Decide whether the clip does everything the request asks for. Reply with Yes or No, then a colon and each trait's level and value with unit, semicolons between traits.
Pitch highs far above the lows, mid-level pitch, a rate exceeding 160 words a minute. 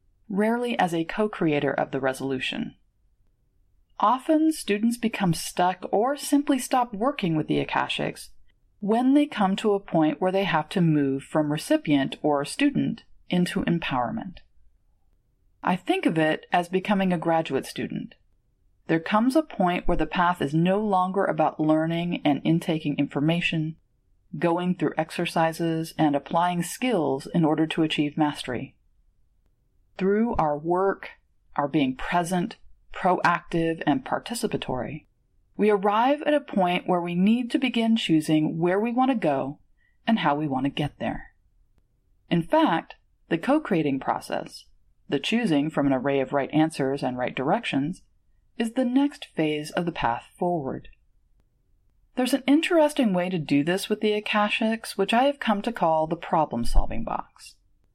No: wide, 6.7 semitones; medium, 170 Hz; average, 155 wpm